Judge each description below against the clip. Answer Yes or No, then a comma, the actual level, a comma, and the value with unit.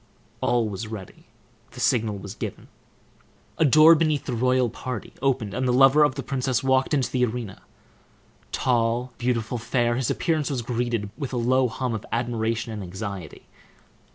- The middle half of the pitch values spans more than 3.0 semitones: No, average, 2.7 semitones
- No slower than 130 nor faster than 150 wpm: No, average, 165 wpm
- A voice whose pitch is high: No, low, 120 Hz